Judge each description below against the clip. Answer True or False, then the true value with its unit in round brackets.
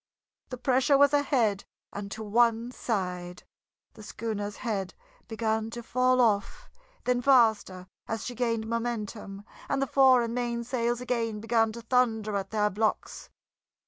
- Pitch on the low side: False (230 Hz)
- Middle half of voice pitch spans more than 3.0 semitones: False (2.7 semitones)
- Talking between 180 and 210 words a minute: False (145 wpm)